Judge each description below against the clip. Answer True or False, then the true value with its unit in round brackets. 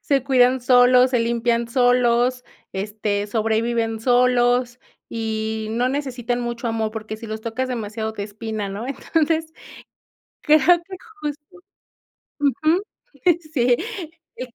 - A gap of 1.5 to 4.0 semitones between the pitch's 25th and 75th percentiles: True (2.6 semitones)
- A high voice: True (240 Hz)